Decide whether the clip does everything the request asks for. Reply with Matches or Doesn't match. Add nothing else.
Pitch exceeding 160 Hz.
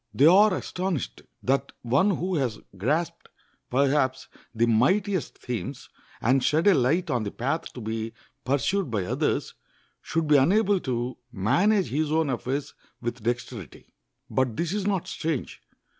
Doesn't match